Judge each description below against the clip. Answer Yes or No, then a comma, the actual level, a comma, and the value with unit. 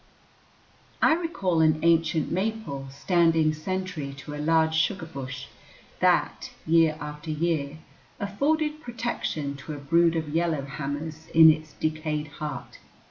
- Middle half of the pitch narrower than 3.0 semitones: Yes, narrow, 2.5 semitones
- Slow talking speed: Yes, slow, 130 wpm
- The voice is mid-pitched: Yes, medium, 160 Hz